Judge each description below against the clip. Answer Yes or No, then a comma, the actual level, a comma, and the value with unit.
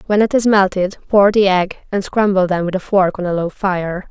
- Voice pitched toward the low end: No, high, 190 Hz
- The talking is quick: Yes, fast, 250 wpm